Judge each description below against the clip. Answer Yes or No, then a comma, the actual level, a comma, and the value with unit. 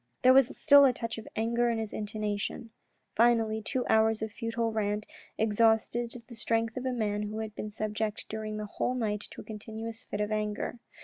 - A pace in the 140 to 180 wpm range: No, average, 195 wpm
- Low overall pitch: No, high, 220 Hz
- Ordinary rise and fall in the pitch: No, narrow, 1.6 semitones